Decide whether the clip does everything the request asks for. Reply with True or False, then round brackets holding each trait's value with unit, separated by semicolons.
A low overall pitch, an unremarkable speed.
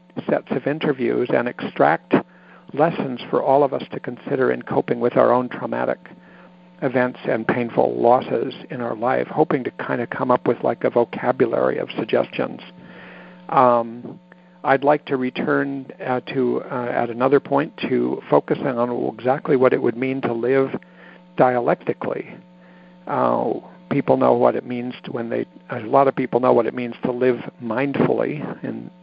True (125 Hz; 165 wpm)